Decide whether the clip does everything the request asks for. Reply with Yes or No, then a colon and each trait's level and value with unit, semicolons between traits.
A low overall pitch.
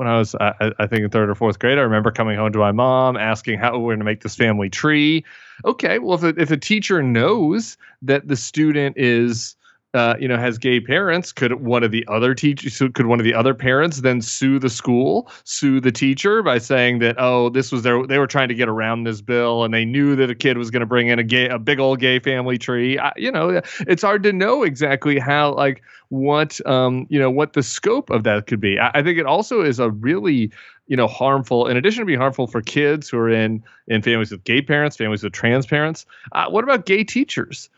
Yes: low, 125 Hz